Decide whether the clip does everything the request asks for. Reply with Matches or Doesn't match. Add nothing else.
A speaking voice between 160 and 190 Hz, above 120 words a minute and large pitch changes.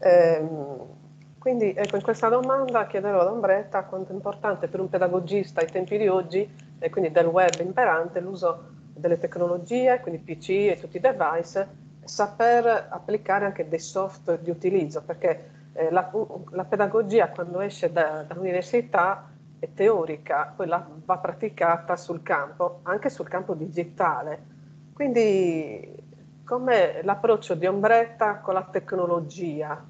Doesn't match